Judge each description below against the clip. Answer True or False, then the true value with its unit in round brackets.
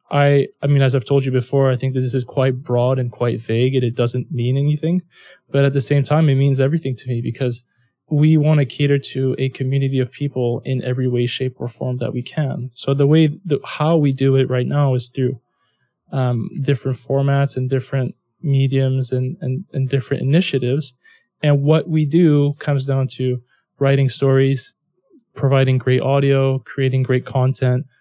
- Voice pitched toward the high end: False (135 Hz)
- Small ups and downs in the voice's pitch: True (1.8 semitones)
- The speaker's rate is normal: True (190 wpm)